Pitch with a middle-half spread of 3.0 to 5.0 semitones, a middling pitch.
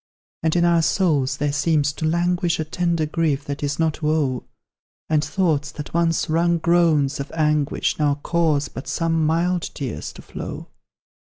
No: narrow, 2.5 semitones; medium, 155 Hz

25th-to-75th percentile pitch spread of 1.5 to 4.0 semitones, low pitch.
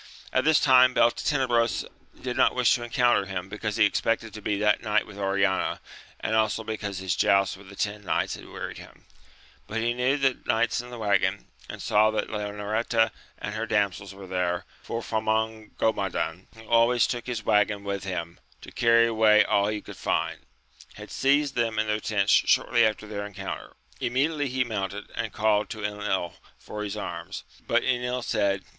Yes: average, 2.7 semitones; low, 110 Hz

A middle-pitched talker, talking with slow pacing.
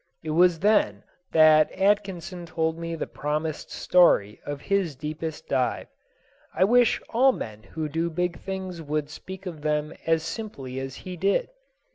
No: medium, 165 Hz; average, 155 wpm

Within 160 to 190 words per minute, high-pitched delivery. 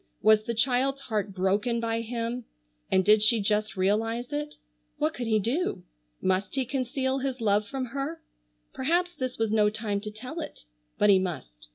Yes: average, 180 wpm; high, 230 Hz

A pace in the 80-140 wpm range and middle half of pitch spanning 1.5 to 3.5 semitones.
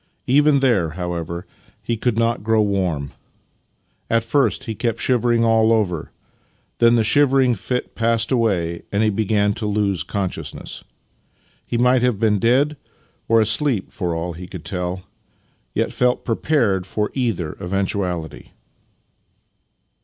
No: slow, 135 wpm; average, 4.4 semitones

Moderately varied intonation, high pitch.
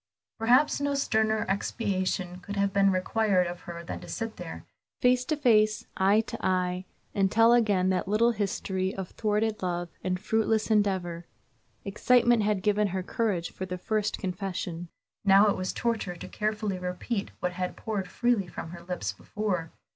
Yes: average, 3.2 semitones; high, 200 Hz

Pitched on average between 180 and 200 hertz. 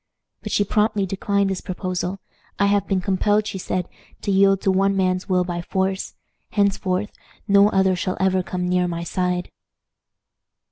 Yes: high, 190 Hz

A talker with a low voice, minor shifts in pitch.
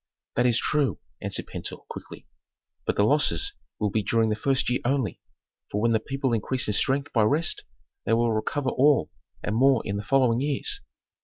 No: low, 125 Hz; average, 3.9 semitones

